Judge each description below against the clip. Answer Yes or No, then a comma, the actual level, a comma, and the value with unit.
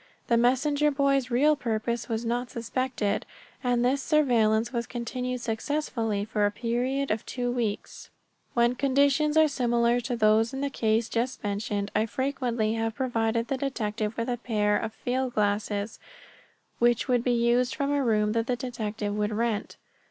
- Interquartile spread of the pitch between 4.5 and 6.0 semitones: No, average, 2.8 semitones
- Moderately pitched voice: No, high, 235 Hz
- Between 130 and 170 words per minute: Yes, average, 165 wpm